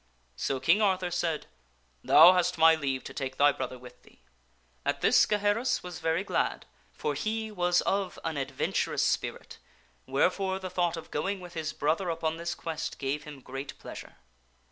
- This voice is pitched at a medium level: Yes, medium, 165 Hz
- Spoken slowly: No, average, 175 wpm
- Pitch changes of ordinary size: Yes, average, 4.5 semitones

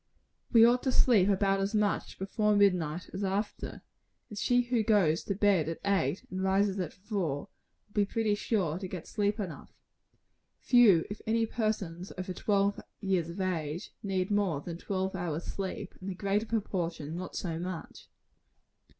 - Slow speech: No, average, 165 wpm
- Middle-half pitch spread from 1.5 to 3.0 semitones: Yes, average, 2.7 semitones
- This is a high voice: Yes, high, 195 Hz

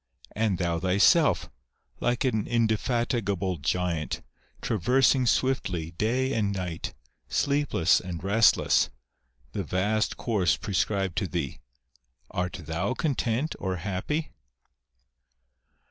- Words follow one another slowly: Yes, slow, 100 wpm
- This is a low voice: Yes, low, 100 Hz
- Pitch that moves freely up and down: No, average, 4.9 semitones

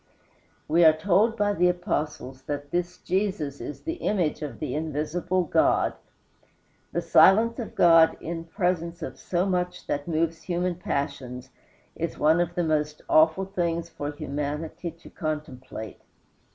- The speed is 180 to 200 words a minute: No, average, 145 wpm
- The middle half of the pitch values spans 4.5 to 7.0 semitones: No, average, 3.0 semitones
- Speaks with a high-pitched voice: No, medium, 165 Hz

